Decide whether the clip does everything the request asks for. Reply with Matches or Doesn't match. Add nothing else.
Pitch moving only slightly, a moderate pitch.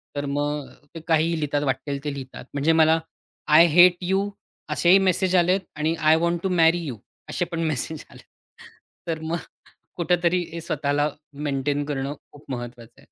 Doesn't match